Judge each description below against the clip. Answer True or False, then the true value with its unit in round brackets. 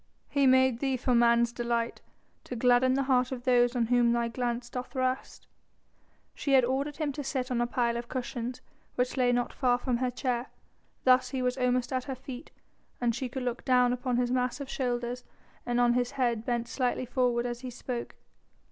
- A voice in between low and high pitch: False (250 Hz)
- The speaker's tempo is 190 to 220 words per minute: True (200 wpm)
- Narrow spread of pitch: True (1.2 semitones)